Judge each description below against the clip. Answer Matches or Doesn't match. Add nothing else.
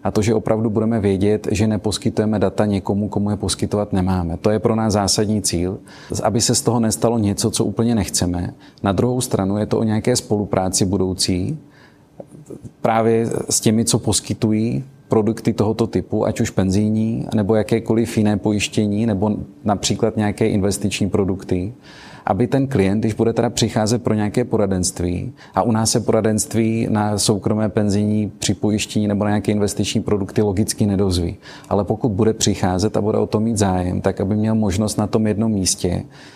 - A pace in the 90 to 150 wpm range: Doesn't match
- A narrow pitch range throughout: Matches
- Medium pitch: Doesn't match